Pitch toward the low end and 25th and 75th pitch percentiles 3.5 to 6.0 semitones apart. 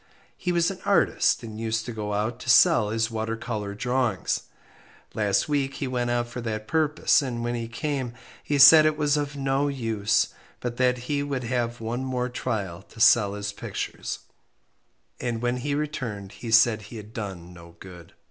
Yes: low, 120 Hz; average, 3.8 semitones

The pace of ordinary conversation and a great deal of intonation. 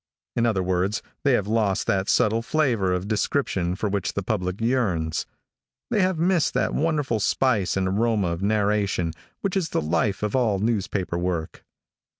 No: average, 165 wpm; average, 4.2 semitones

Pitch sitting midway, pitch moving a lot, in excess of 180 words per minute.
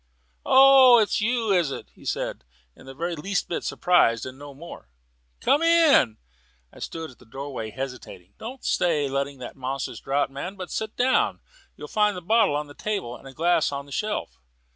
Yes: medium, 160 Hz; wide, 7.8 semitones; average, 195 wpm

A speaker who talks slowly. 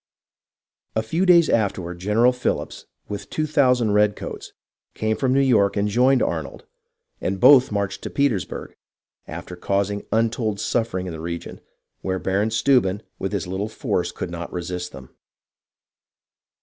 No: average, 145 wpm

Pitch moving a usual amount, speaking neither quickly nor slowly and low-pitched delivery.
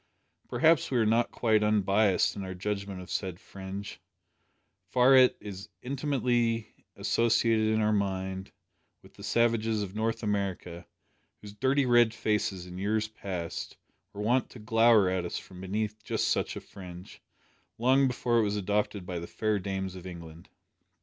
Yes: average, 3.3 semitones; average, 165 wpm; low, 105 Hz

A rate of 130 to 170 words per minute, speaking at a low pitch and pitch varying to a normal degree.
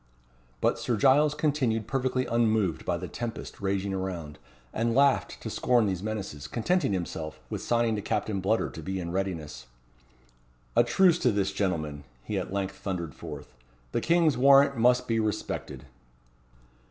Yes: average, 155 wpm; low, 110 Hz; average, 5.0 semitones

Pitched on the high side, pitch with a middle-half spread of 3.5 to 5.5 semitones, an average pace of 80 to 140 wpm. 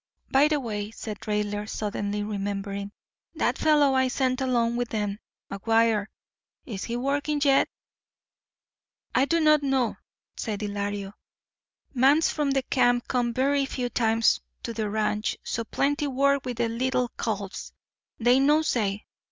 Yes: high, 240 Hz; average, 4.5 semitones; slow, 135 wpm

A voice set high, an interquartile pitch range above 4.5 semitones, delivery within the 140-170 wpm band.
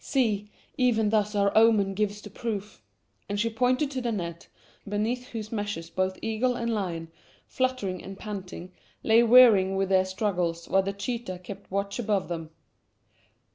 No: high, 205 Hz; average, 3.3 semitones; average, 160 wpm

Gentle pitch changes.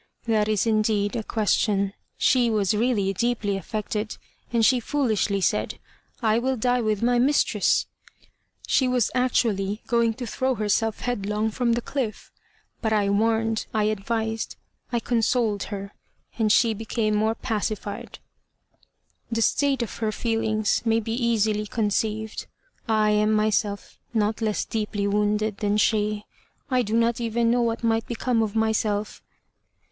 Yes: narrow, 1.8 semitones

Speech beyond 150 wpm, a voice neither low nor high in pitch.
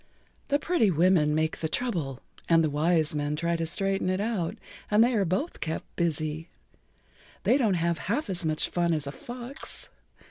Yes: average, 180 wpm; medium, 170 Hz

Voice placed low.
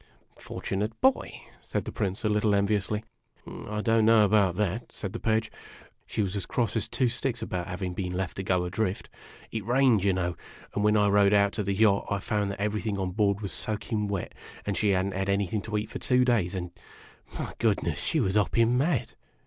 Yes: low, 105 Hz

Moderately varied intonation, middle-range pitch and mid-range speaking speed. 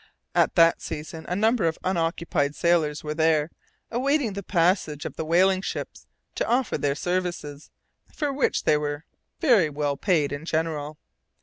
Yes: average, 3.9 semitones; medium, 165 Hz; average, 160 wpm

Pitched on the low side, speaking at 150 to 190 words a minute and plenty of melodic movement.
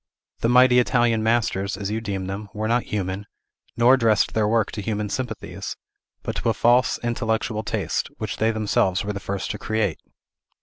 No: low, 110 Hz; average, 180 wpm; narrow, 2.4 semitones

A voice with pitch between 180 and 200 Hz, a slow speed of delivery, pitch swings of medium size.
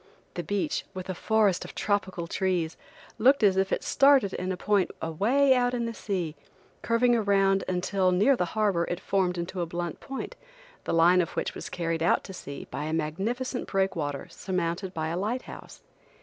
No: high, 190 Hz; average, 190 wpm; average, 3.9 semitones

